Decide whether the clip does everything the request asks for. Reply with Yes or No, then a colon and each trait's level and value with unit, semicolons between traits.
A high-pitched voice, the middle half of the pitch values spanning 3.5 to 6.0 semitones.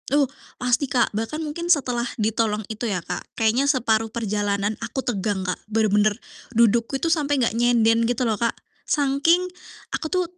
Yes: high, 230 Hz; average, 3.9 semitones